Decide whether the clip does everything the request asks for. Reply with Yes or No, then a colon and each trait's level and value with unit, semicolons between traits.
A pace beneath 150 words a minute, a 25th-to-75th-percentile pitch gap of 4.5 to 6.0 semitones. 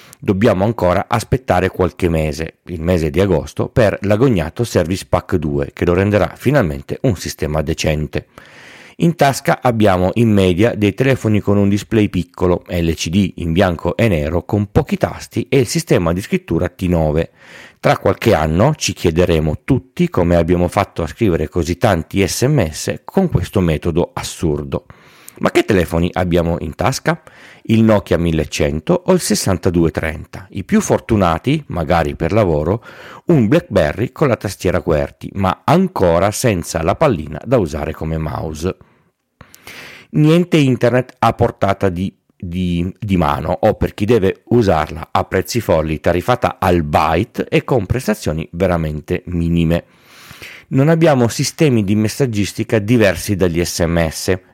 Yes: average, 140 wpm; wide, 5.6 semitones